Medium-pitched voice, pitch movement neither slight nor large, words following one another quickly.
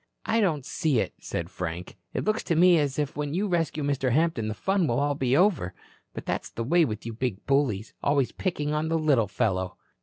No: medium, 145 Hz; wide, 6.0 semitones; fast, 220 wpm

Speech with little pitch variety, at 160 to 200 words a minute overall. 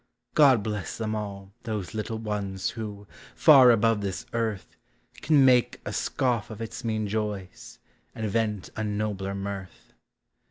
No: narrow, 2.3 semitones; average, 145 wpm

